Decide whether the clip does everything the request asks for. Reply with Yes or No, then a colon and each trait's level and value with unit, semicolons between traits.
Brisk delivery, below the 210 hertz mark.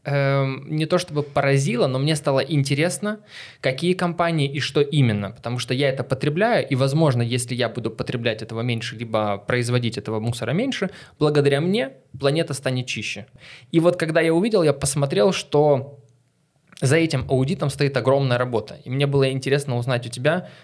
Yes: fast, 170 wpm; medium, 140 Hz